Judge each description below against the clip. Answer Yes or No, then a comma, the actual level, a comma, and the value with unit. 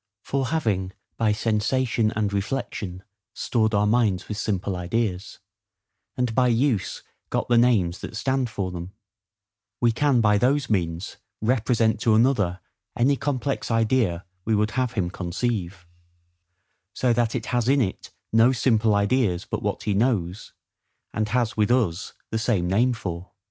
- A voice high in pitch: No, low, 110 Hz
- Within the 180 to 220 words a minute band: No, average, 150 wpm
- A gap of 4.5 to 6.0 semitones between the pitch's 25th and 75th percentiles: No, average, 3.8 semitones